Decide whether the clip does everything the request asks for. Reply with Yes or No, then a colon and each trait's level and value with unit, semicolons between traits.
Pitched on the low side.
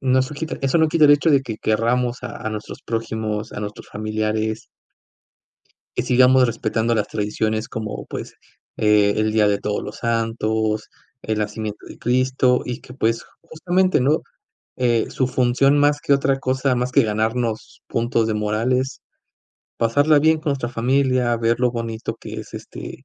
Yes: low, 120 Hz